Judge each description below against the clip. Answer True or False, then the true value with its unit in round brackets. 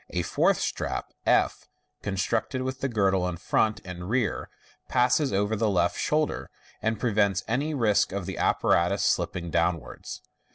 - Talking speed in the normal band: True (150 wpm)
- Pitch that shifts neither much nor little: True (4.9 semitones)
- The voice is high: False (105 Hz)